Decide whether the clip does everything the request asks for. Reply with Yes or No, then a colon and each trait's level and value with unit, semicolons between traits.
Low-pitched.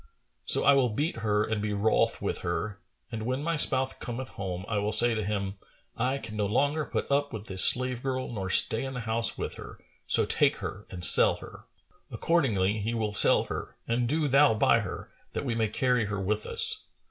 Yes: low, 115 Hz